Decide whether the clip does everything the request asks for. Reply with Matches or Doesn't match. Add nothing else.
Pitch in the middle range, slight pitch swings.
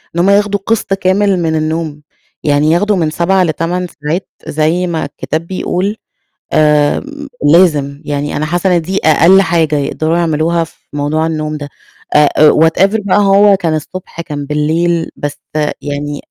Doesn't match